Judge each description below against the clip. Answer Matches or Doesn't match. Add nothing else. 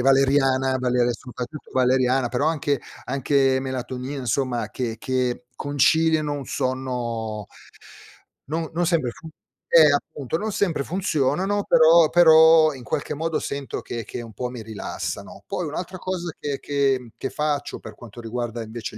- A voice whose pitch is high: Doesn't match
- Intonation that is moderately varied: Matches